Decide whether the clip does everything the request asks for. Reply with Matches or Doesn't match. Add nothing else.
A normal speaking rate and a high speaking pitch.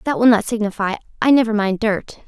Doesn't match